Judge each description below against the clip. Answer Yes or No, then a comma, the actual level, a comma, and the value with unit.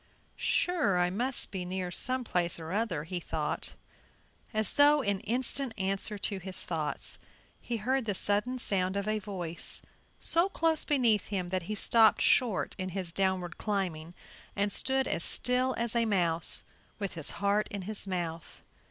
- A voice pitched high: Yes, high, 200 Hz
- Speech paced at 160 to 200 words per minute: Yes, average, 165 wpm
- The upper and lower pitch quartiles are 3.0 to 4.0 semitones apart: No, average, 4.5 semitones